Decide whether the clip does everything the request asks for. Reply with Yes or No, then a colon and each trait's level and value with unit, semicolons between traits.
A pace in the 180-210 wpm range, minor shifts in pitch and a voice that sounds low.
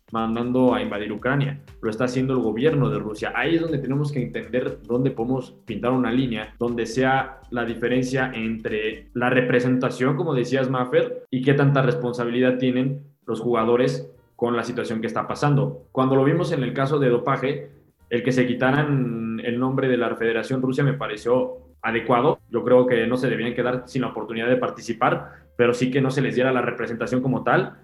Yes: fast, 190 wpm; narrow, 2.0 semitones; low, 125 Hz